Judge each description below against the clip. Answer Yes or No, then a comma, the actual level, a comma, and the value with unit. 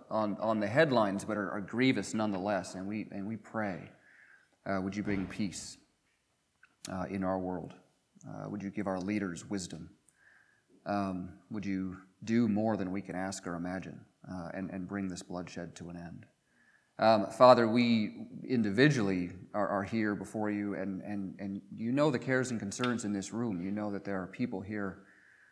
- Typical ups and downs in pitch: No, narrow, 2.2 semitones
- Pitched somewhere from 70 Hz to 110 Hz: Yes, low, 100 Hz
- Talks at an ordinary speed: Yes, average, 185 wpm